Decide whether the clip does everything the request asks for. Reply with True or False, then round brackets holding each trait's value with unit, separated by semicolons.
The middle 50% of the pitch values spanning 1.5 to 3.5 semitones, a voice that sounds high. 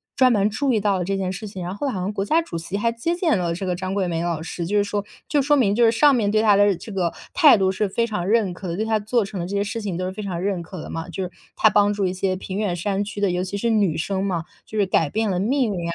True (3.0 semitones; 200 Hz)